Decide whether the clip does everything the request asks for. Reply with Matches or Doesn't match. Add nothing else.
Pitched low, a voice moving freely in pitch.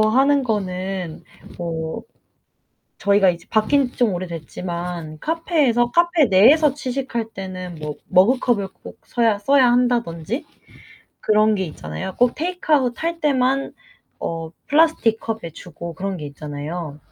Doesn't match